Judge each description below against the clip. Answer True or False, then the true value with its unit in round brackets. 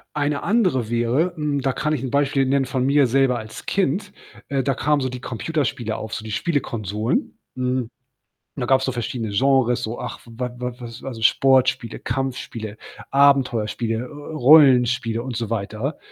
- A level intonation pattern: False (3.0 semitones)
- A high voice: False (130 Hz)